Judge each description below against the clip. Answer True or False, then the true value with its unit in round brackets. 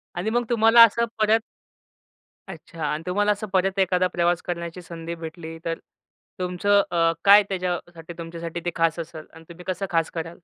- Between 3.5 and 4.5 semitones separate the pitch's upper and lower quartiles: False (3.0 semitones)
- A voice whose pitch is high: False (175 Hz)